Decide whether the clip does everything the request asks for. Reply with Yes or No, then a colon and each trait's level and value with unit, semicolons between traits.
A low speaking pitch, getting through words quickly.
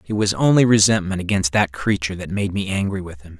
Yes: very low, 95 Hz; fast, 230 wpm